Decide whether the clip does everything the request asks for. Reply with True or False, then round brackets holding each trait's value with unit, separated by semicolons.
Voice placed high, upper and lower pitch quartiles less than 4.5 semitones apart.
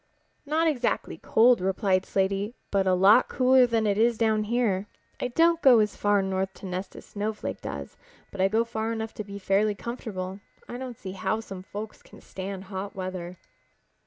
True (205 Hz; 3.2 semitones)